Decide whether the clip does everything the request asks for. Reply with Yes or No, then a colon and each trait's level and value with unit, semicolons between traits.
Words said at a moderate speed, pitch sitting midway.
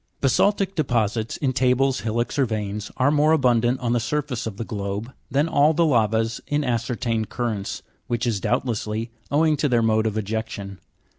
No: average, 170 wpm; low, 120 Hz